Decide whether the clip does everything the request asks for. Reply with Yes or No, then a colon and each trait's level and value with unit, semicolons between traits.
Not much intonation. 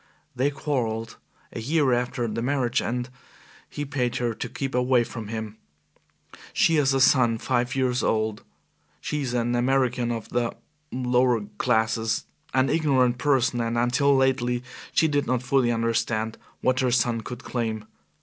Yes: narrow, 2.3 semitones